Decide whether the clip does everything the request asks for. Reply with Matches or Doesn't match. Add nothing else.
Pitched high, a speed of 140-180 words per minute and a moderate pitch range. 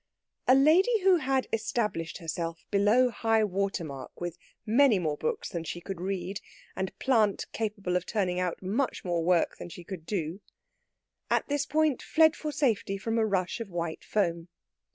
Doesn't match